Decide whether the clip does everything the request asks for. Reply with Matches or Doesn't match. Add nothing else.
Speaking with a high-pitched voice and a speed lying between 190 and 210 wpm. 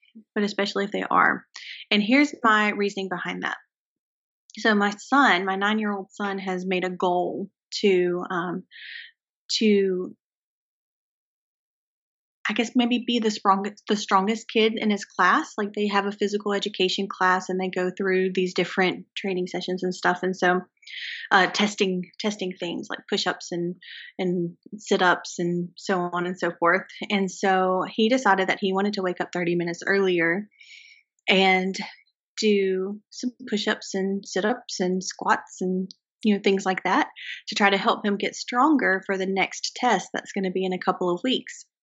Doesn't match